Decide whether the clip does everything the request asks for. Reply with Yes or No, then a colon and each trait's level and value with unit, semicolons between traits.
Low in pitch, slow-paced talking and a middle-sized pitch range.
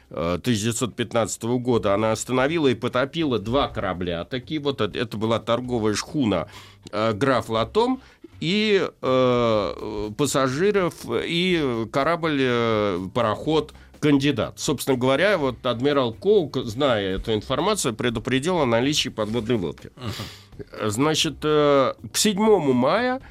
Yes: low, 125 Hz; slow, 105 wpm; average, 4.8 semitones